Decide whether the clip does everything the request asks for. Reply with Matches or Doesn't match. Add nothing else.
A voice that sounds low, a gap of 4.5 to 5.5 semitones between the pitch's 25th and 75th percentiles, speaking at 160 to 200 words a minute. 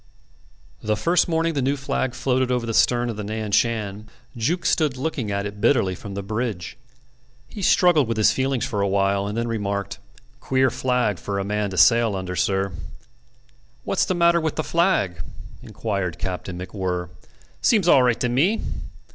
Matches